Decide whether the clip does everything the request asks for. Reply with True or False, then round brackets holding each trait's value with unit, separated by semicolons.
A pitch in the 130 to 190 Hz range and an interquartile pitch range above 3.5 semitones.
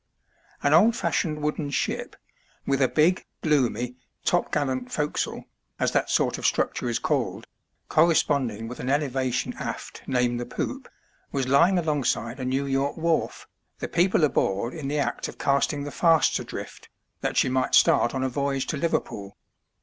False (140 Hz; 3.1 semitones)